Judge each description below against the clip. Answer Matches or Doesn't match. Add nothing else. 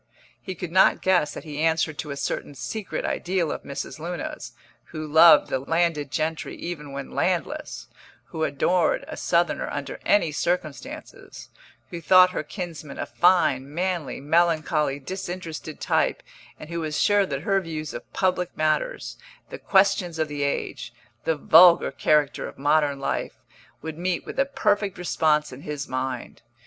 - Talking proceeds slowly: Doesn't match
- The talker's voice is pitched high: Doesn't match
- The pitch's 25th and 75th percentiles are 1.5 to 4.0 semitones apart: Matches